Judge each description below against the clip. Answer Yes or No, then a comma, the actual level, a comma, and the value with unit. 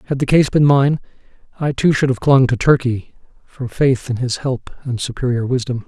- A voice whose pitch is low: Yes, low, 130 Hz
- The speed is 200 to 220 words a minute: Yes, fast, 205 wpm